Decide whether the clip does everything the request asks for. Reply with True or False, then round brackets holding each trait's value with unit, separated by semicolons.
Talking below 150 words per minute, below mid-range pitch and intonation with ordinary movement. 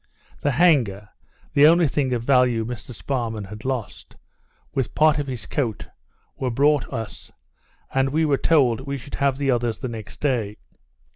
False (165 wpm; 130 Hz; 3.7 semitones)